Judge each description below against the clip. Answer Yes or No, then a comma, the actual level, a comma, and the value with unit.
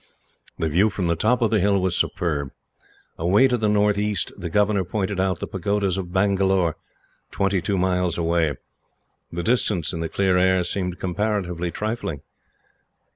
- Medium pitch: No, very low, 95 Hz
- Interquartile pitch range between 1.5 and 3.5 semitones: Yes, average, 2.9 semitones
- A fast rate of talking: No, average, 160 wpm